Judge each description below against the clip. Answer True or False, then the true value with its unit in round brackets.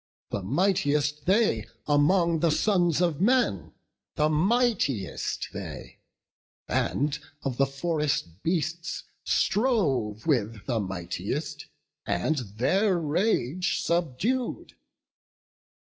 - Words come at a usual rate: False (90 wpm)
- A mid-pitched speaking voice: True (150 Hz)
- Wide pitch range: True (6.3 semitones)